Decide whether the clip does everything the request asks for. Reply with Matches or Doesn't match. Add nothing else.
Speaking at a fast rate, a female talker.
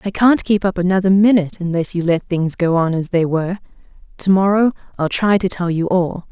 Matches